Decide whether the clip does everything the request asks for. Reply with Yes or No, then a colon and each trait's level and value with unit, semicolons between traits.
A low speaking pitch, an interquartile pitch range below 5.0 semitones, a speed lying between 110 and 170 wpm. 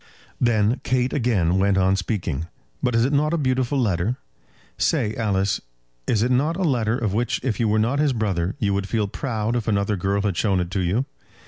No: low, 110 Hz; average, 4.1 semitones; fast, 205 wpm